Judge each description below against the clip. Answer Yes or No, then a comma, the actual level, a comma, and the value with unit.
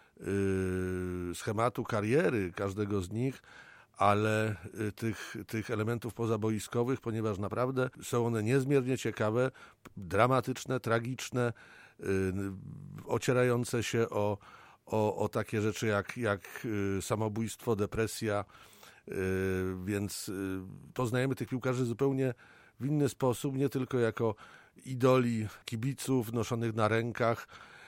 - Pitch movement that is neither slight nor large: Yes, average, 3.4 semitones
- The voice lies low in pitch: Yes, low, 115 Hz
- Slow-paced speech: Yes, slow, 95 wpm